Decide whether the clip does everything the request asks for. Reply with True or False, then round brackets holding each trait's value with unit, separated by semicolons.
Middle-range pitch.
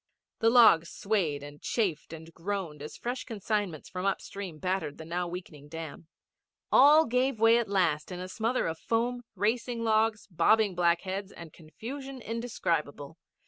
False (195 Hz)